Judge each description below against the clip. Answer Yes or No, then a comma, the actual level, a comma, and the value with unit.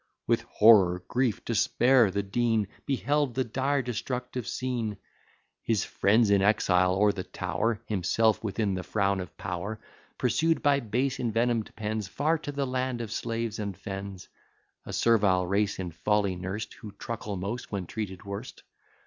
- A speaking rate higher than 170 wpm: No, average, 155 wpm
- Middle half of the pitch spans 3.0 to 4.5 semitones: Yes, average, 3.7 semitones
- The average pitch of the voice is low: Yes, low, 110 Hz